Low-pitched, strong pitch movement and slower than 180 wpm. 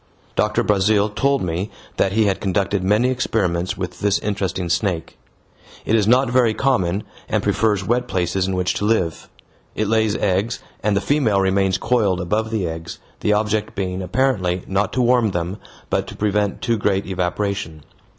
No: low, 100 Hz; average, 3.0 semitones; average, 170 wpm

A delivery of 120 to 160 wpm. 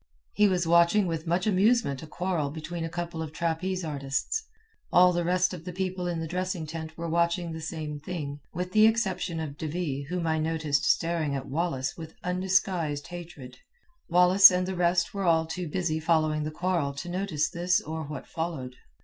No: average, 190 wpm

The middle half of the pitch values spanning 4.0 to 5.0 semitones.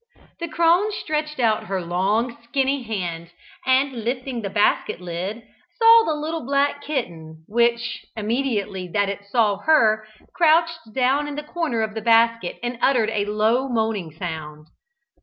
No: wide, 5.6 semitones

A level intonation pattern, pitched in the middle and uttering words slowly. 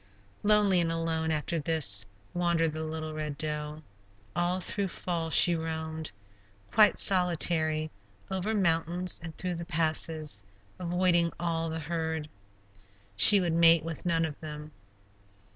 Yes: narrow, 1.8 semitones; medium, 165 Hz; slow, 130 wpm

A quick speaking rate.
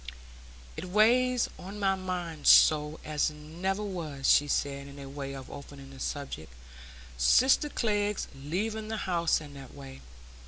No: average, 145 wpm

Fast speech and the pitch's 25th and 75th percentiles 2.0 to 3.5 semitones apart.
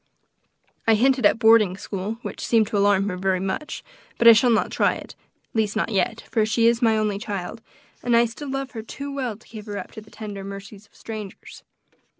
Yes: fast, 225 wpm; narrow, 2.4 semitones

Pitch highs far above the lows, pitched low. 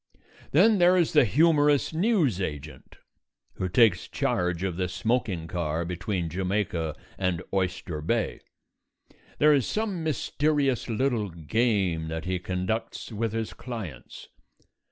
Yes: wide, 7.7 semitones; low, 105 Hz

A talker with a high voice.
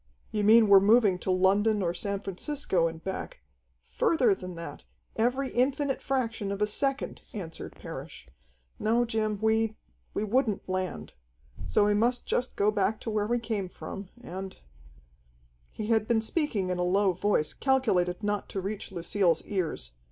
Yes: high, 205 Hz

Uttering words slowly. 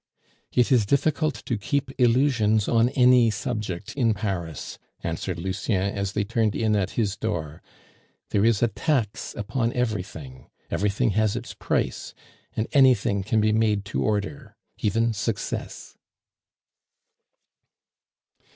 Yes: slow, 125 wpm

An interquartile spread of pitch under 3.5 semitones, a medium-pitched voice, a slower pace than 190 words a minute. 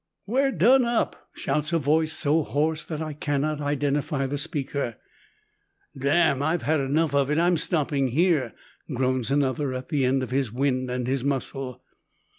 Yes: average, 2.9 semitones; medium, 145 Hz; average, 160 wpm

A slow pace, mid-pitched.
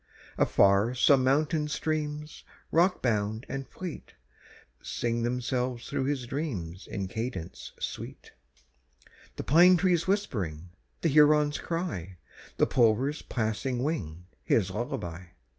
No: slow, 110 wpm; low, 130 Hz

